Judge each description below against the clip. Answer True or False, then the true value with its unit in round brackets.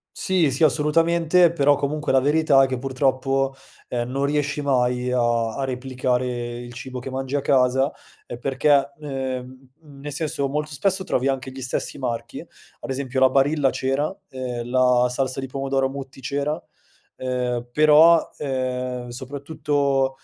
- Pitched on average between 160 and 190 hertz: False (135 Hz)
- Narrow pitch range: True (2.1 semitones)